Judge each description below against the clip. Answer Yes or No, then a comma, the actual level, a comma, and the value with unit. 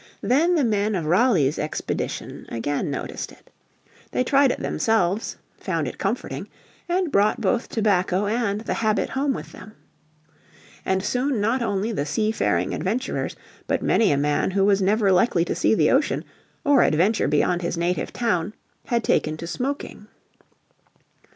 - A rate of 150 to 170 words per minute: Yes, average, 155 wpm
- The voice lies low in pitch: No, high, 210 Hz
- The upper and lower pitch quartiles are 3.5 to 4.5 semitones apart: No, average, 5.1 semitones